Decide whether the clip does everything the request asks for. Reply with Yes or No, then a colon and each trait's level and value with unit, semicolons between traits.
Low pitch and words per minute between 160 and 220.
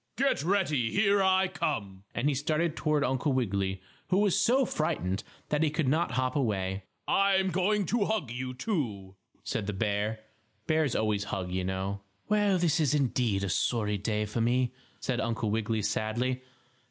Yes: low, 130 Hz; average, 170 wpm